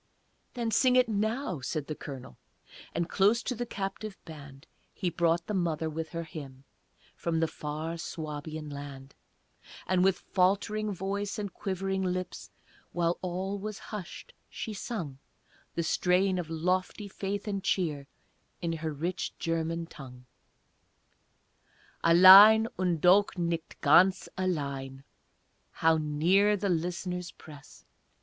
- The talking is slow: Yes, slow, 130 wpm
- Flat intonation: No, average, 3.7 semitones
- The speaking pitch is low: No, medium, 175 Hz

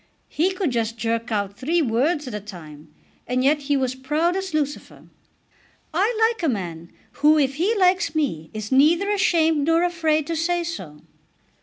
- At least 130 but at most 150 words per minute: No, average, 175 wpm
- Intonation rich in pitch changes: Yes, wide, 6.9 semitones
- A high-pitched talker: Yes, very high, 295 Hz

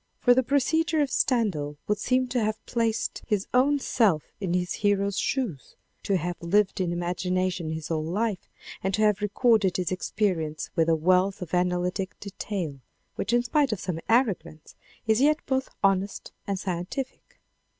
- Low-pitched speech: No, high, 195 Hz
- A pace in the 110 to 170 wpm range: Yes, average, 165 wpm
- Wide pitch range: No, average, 4.6 semitones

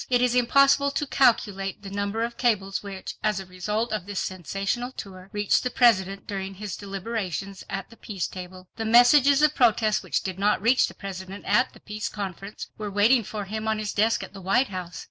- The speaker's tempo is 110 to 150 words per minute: No, fast, 205 wpm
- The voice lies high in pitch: Yes, high, 205 Hz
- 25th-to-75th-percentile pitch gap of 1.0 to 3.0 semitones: No, average, 3.4 semitones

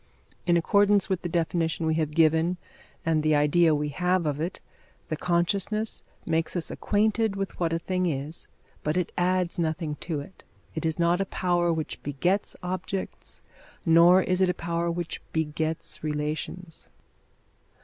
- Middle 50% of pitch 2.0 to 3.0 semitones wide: Yes, narrow, 2.4 semitones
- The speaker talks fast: No, average, 160 wpm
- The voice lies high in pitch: No, medium, 170 Hz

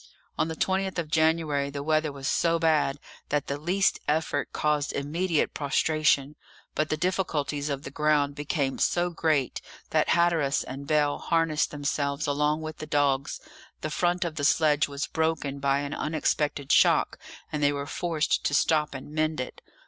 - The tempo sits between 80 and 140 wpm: No, average, 170 wpm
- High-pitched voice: No, medium, 150 Hz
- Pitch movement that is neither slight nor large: No, narrow, 2.0 semitones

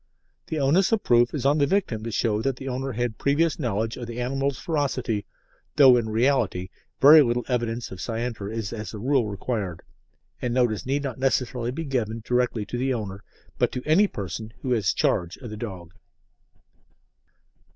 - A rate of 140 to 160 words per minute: No, average, 180 wpm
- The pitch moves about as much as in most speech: Yes, average, 3.7 semitones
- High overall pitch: No, low, 120 Hz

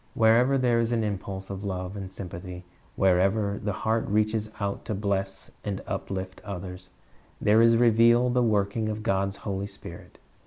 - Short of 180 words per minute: Yes, average, 165 wpm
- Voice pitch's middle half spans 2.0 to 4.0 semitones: Yes, average, 2.7 semitones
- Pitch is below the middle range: Yes, low, 100 Hz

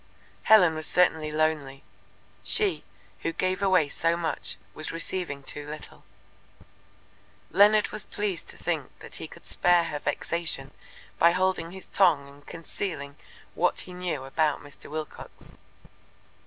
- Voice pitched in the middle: Yes, medium, 165 Hz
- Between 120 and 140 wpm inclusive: Yes, slow, 135 wpm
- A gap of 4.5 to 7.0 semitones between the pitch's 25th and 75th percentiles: No, average, 3.6 semitones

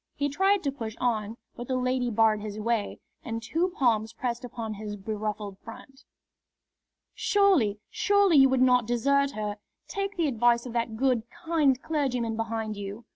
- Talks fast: No, average, 165 wpm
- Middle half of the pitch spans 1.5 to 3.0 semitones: No, average, 4.2 semitones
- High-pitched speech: Yes, high, 240 Hz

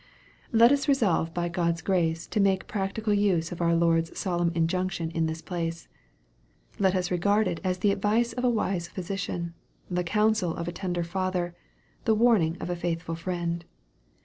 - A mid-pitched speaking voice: Yes, medium, 180 Hz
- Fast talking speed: No, average, 175 wpm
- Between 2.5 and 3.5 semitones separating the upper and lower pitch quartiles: Yes, average, 2.9 semitones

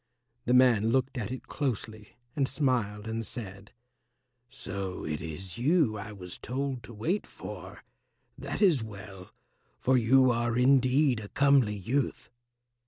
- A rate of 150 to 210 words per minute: No, average, 140 wpm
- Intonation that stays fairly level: No, average, 4.1 semitones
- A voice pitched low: Yes, low, 120 Hz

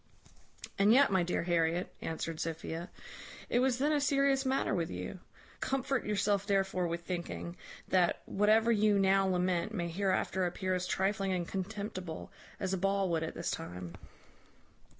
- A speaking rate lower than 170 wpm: Yes, average, 155 wpm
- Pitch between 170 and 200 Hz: Yes, high, 190 Hz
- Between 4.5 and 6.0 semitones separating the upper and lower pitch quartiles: No, average, 3.5 semitones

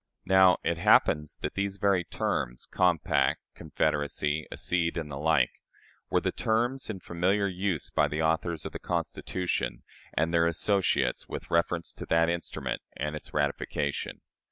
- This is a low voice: Yes, very low, 85 Hz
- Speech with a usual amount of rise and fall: Yes, average, 3.5 semitones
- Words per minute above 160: No, average, 150 wpm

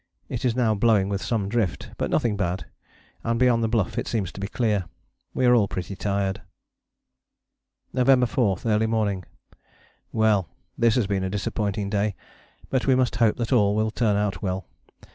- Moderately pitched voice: No, low, 105 Hz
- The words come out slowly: No, average, 180 wpm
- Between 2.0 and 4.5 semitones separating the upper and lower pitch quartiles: Yes, average, 2.8 semitones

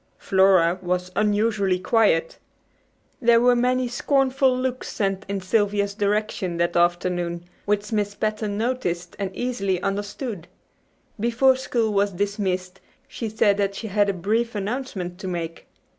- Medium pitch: No, high, 205 Hz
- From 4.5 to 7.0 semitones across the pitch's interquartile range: No, average, 3.7 semitones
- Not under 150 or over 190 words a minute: No, slow, 135 wpm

